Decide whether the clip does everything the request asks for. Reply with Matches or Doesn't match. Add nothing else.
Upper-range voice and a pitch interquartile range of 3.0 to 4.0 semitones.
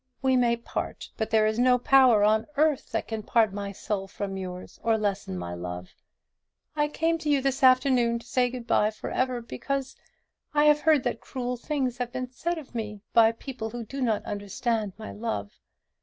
Matches